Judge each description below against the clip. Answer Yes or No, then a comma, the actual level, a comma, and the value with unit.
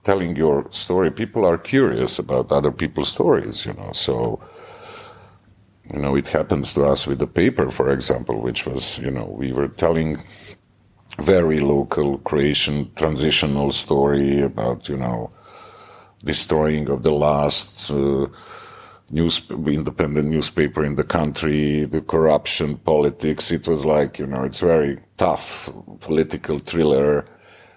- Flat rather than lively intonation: Yes, narrow, 2.1 semitones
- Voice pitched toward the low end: Yes, very low, 75 Hz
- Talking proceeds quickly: No, slow, 135 wpm